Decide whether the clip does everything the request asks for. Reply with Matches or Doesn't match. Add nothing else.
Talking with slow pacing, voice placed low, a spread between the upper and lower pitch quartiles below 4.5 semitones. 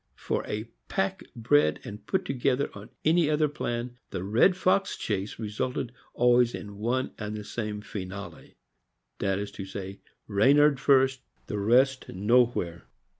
Doesn't match